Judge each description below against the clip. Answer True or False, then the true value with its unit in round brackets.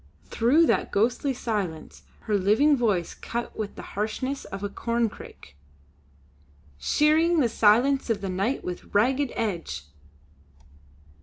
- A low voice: False (225 Hz)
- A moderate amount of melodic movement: True (5.0 semitones)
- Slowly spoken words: True (125 wpm)